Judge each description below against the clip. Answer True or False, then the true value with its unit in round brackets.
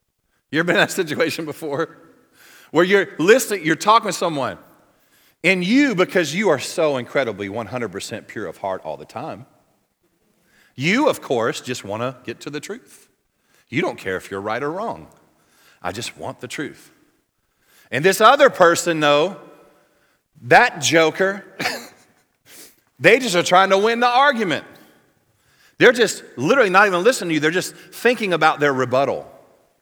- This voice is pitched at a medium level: True (180 Hz)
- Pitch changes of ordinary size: False (6.7 semitones)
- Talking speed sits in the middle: True (160 wpm)